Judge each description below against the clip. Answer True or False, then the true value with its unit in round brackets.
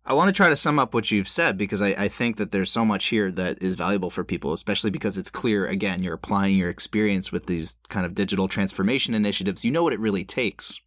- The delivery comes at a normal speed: False (255 wpm)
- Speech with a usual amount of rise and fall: False (1.8 semitones)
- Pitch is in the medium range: False (100 Hz)